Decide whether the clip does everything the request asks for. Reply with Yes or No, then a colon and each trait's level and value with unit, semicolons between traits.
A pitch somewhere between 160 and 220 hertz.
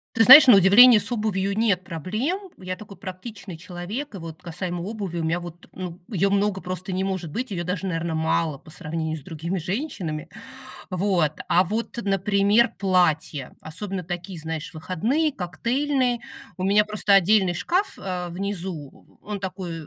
Yes: medium, 185 Hz